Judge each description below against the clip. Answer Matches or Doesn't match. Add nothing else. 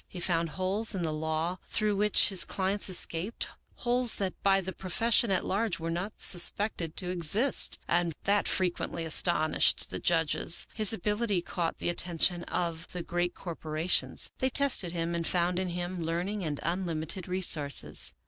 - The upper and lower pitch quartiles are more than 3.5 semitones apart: Doesn't match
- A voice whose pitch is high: Doesn't match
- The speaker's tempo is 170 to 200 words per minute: Doesn't match